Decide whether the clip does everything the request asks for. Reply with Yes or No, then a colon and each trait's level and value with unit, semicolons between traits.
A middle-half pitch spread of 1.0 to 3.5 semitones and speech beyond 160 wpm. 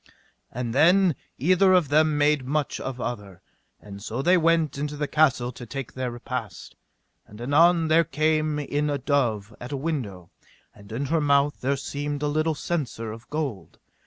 No: average, 4.3 semitones; average, 175 wpm